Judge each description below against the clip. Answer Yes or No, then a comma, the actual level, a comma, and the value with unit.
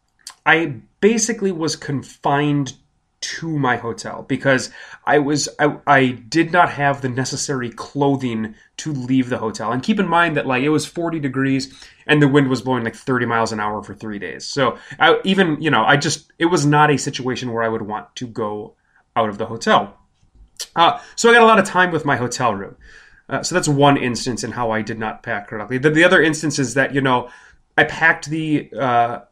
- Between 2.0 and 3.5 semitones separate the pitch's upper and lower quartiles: No, average, 4.2 semitones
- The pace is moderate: No, fast, 210 wpm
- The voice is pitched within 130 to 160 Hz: Yes, low, 135 Hz